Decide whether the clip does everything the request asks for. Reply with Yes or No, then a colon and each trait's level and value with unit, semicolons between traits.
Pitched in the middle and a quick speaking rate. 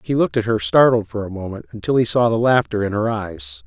No: low, 115 Hz; fast, 260 wpm